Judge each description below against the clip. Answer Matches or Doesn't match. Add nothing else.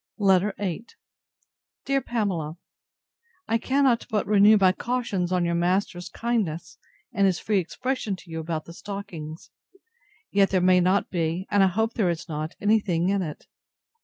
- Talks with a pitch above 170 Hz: Matches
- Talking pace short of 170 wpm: Matches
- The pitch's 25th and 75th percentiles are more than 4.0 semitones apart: Doesn't match